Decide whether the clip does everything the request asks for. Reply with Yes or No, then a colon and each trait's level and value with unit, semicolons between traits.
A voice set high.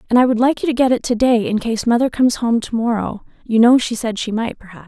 Yes: high, 235 Hz